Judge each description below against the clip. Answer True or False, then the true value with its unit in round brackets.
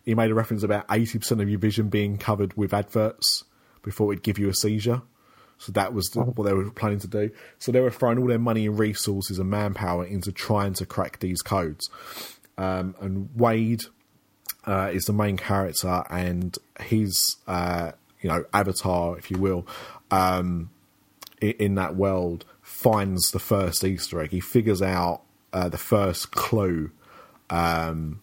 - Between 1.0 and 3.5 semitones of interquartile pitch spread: True (2.7 semitones)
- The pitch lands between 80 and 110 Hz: True (100 Hz)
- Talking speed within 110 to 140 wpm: False (170 wpm)